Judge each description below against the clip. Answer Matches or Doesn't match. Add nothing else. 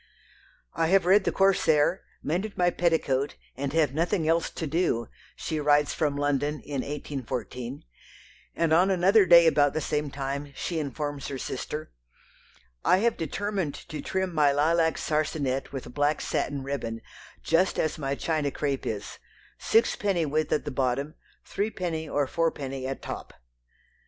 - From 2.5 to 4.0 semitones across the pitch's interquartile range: Matches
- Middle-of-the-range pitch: Matches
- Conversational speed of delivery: Matches